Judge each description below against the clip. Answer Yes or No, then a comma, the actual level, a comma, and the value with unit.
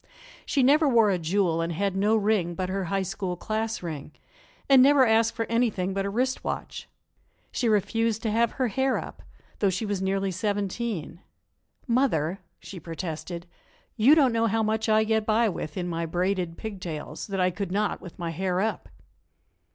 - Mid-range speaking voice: No, high, 200 Hz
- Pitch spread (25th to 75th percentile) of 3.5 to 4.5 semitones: Yes, average, 3.9 semitones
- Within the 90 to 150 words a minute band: No, average, 180 wpm